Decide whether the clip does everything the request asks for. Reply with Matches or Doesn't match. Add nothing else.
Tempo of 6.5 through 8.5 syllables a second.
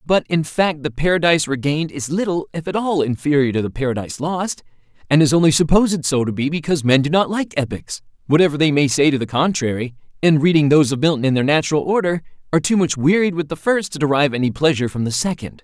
Matches